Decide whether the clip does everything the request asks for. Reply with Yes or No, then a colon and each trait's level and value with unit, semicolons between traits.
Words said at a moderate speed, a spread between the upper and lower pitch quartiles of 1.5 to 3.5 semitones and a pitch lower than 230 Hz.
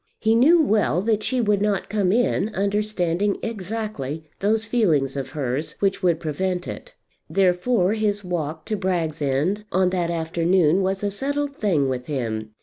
No: average, 160 wpm; average, 4.8 semitones; high, 190 Hz